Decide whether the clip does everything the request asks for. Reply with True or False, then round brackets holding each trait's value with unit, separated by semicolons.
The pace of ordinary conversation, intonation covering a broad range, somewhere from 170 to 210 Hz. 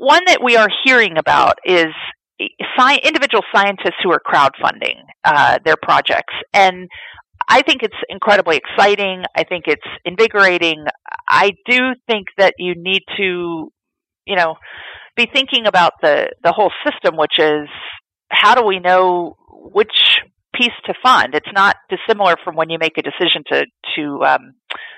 True (155 wpm; 6.0 semitones; 190 Hz)